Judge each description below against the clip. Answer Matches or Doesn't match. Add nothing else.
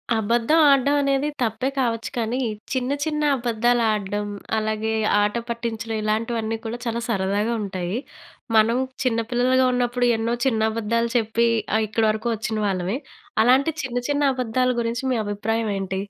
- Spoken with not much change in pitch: Matches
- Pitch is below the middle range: Doesn't match